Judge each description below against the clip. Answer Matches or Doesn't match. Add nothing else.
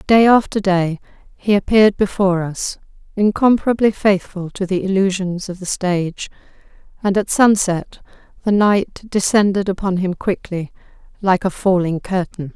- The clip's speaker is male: Doesn't match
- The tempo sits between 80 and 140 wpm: Matches